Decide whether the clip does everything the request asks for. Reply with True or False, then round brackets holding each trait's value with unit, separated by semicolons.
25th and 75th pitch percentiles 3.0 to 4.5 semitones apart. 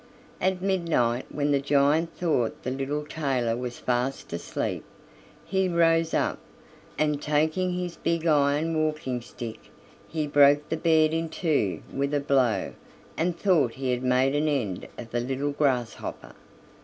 True (4.1 semitones)